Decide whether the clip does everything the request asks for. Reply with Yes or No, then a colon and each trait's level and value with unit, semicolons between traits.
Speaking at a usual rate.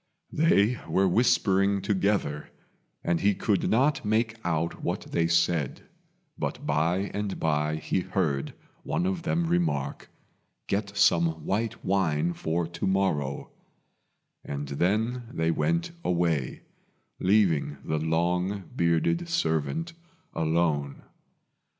No: slow, 115 wpm